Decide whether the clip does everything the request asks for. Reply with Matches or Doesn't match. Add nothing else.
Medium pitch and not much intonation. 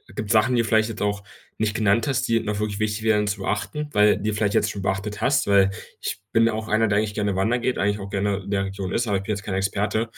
Doesn't match